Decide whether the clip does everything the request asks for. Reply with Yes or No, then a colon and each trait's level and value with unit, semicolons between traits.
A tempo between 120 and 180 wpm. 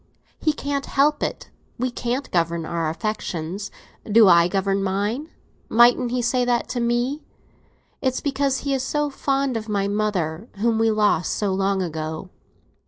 Yes: average, 160 wpm